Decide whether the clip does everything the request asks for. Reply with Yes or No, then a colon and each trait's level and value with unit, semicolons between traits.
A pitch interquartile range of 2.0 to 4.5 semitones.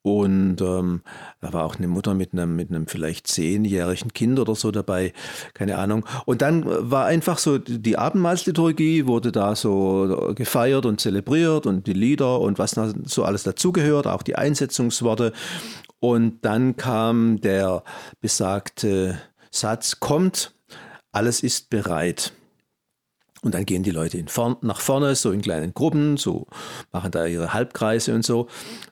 No: average, 5.1 semitones